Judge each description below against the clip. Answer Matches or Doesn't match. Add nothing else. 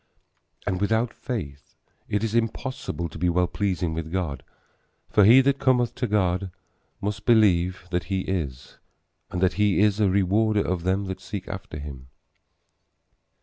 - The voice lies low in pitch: Matches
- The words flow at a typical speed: Matches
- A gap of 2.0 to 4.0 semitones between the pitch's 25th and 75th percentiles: Matches